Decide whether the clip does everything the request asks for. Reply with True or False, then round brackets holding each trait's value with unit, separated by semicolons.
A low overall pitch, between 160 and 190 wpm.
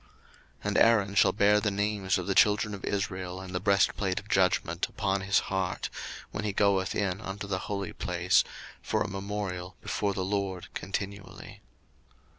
True (100 Hz; 170 wpm)